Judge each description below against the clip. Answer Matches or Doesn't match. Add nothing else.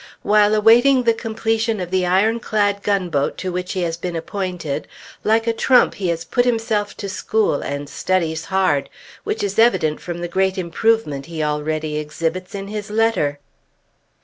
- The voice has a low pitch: Doesn't match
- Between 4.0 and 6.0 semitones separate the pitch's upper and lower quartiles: Matches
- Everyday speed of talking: Matches